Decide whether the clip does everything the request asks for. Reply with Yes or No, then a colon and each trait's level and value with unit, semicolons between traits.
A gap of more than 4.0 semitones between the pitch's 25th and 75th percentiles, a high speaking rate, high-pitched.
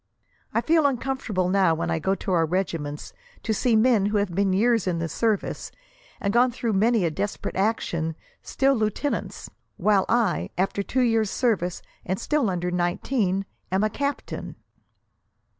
No: average, 4.4 semitones; average, 160 wpm; high, 200 Hz